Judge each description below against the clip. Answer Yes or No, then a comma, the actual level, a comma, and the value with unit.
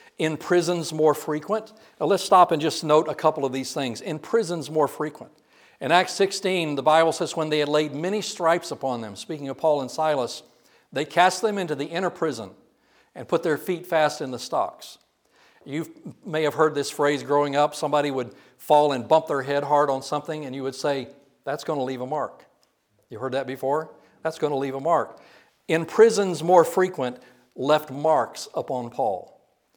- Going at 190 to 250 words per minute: Yes, average, 200 wpm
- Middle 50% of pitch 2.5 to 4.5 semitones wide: Yes, average, 3.1 semitones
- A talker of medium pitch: Yes, medium, 155 Hz